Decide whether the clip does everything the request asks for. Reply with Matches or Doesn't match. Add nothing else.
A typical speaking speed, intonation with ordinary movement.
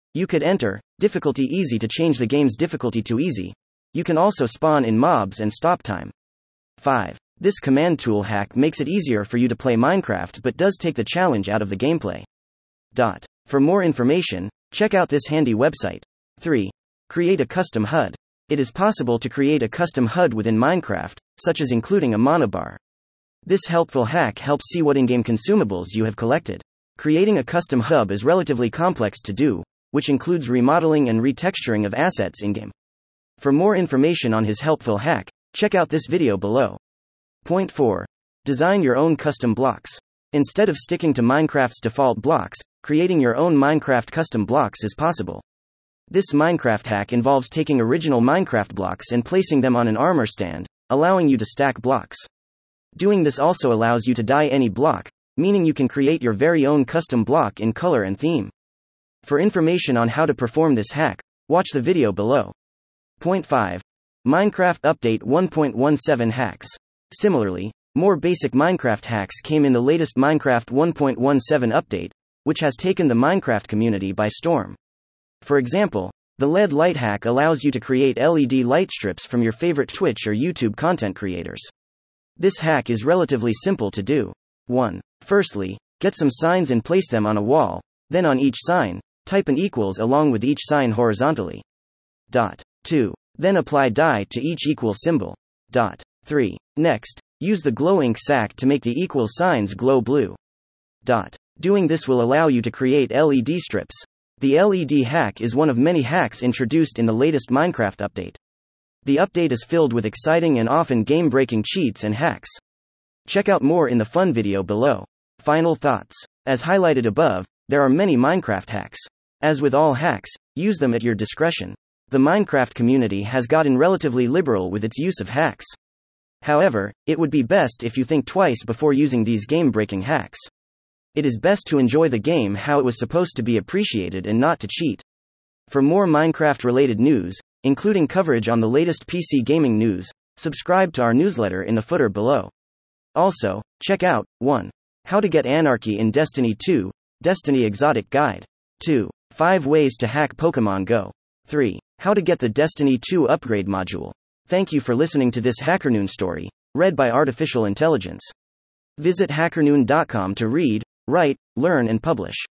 Doesn't match